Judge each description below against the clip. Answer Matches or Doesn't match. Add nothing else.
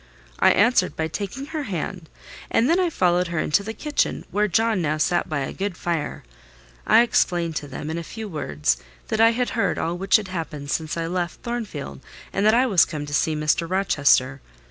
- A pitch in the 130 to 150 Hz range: Doesn't match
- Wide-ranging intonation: Matches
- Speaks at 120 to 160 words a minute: Doesn't match